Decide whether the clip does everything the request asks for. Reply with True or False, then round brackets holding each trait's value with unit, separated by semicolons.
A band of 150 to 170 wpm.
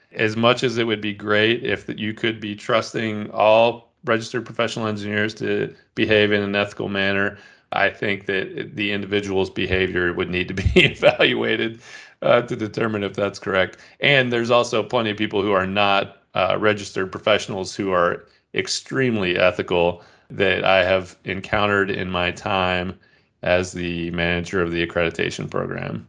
True (160 wpm)